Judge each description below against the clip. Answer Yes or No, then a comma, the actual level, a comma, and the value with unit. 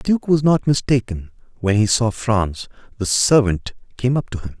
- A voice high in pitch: No, low, 115 Hz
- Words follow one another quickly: No, average, 195 wpm